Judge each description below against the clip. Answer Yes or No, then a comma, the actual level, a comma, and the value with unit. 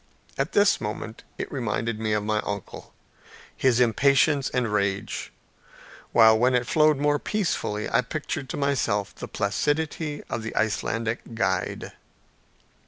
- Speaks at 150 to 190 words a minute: No, slow, 135 wpm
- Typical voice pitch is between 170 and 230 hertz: No, low, 120 Hz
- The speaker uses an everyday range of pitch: Yes, average, 4.8 semitones